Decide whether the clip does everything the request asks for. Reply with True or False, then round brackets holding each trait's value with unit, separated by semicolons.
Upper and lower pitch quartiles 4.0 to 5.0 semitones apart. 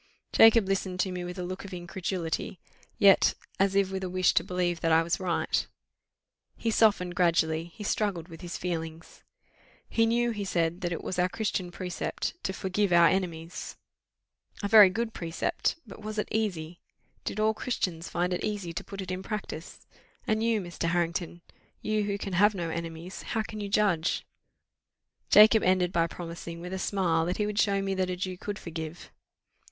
False (3.1 semitones)